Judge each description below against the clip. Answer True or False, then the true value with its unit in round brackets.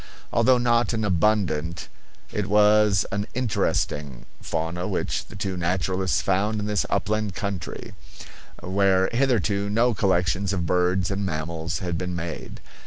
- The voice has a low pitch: True (95 Hz)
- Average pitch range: True (3.1 semitones)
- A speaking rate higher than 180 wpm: False (135 wpm)